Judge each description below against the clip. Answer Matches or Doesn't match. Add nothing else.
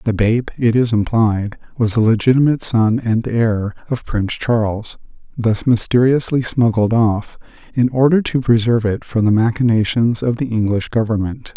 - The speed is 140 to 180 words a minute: Matches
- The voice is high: Doesn't match